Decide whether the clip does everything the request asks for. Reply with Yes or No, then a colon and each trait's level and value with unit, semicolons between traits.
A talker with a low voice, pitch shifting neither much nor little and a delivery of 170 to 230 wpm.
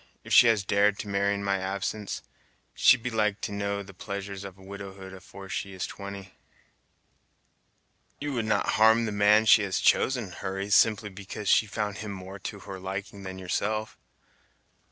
No: low, 100 Hz; narrow, 1.6 semitones; average, 175 wpm